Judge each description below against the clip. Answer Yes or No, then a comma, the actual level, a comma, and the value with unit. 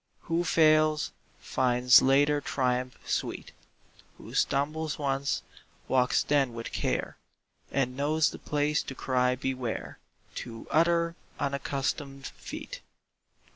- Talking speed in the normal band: No, slow, 105 wpm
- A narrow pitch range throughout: No, average, 3.1 semitones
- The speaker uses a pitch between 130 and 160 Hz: Yes, medium, 140 Hz